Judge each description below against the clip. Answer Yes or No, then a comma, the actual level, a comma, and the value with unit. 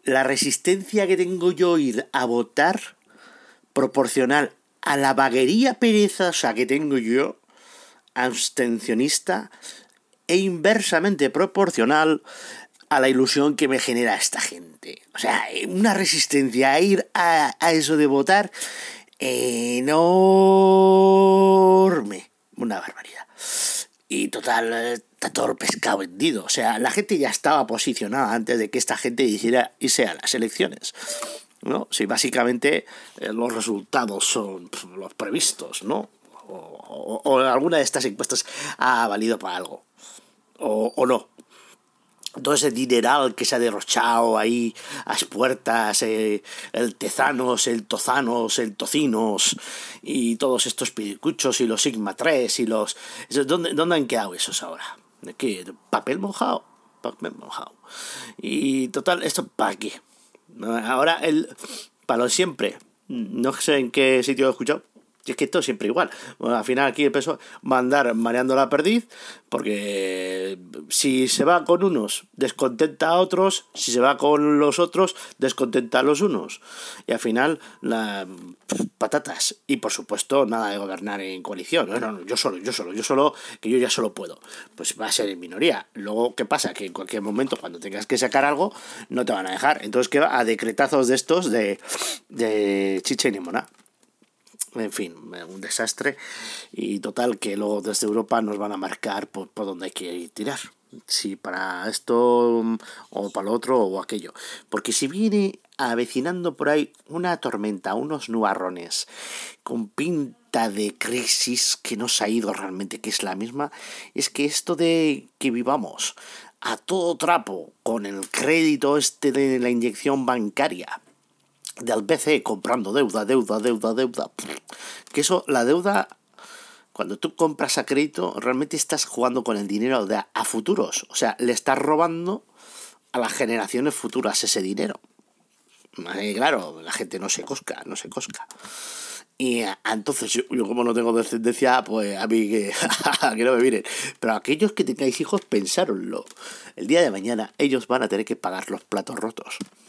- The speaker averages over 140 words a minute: Yes, average, 160 wpm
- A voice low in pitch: Yes, low, 130 Hz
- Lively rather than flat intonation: Yes, wide, 5.8 semitones